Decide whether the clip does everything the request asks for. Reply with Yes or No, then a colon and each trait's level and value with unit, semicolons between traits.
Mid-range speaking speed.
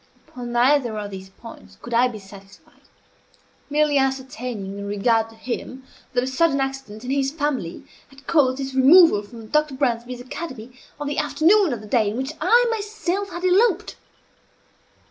Yes: average, 165 wpm